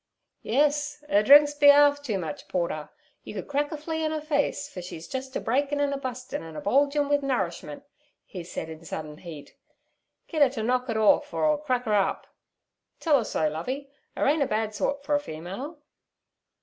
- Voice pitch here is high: Yes, very high, 265 Hz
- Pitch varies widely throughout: Yes, wide, 7.0 semitones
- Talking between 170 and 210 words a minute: Yes, average, 200 wpm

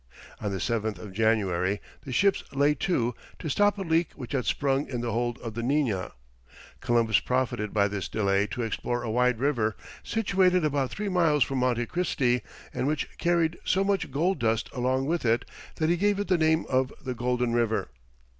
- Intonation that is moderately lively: No, wide, 5.9 semitones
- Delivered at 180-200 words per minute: Yes, average, 190 wpm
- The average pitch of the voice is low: Yes, low, 125 Hz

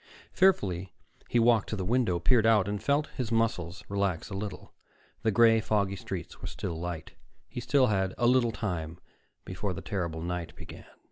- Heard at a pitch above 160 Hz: No, low, 100 Hz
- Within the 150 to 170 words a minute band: No, average, 180 wpm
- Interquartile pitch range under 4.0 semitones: No, average, 4.3 semitones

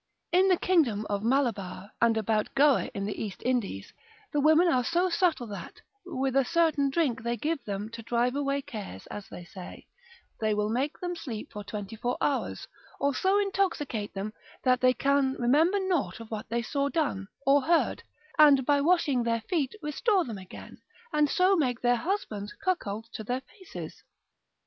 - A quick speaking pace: No, average, 180 wpm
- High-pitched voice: Yes, very high, 260 Hz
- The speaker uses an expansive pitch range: Yes, wide, 6.3 semitones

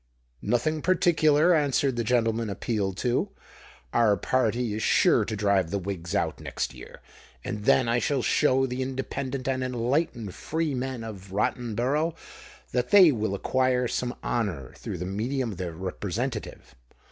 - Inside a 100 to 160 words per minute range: Yes, average, 145 wpm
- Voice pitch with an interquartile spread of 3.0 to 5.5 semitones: Yes, average, 4.2 semitones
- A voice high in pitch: No, low, 120 Hz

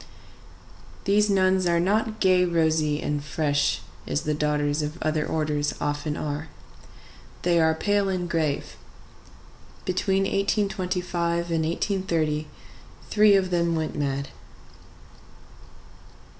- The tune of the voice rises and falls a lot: No, average, 3.7 semitones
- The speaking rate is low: Yes, slow, 110 wpm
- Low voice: No, medium, 170 Hz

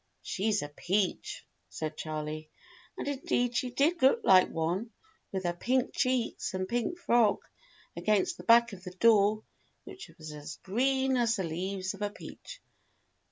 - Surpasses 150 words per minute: Yes, average, 160 wpm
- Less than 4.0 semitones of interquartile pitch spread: No, average, 5.3 semitones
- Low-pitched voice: No, high, 210 Hz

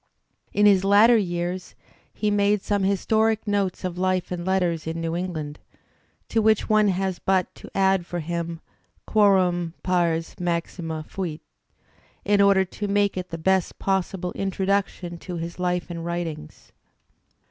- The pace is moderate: Yes, average, 145 wpm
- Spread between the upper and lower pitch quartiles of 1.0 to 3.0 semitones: Yes, narrow, 2.6 semitones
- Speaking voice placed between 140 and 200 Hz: Yes, medium, 185 Hz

